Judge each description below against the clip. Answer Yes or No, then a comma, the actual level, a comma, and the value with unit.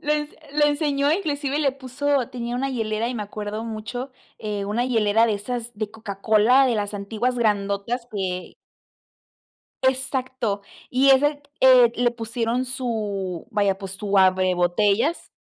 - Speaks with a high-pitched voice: Yes, high, 230 Hz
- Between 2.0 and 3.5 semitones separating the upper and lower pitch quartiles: No, average, 4.2 semitones